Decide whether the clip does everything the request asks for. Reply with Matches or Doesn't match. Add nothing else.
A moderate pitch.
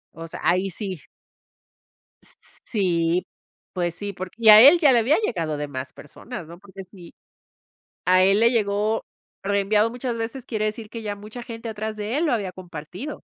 Doesn't match